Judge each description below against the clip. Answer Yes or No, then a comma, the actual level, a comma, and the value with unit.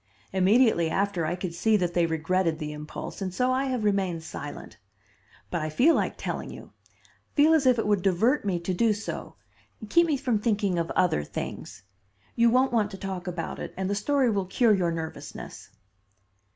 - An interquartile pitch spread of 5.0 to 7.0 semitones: Yes, average, 5.3 semitones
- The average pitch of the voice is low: No, high, 195 Hz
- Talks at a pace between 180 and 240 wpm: Yes, average, 190 wpm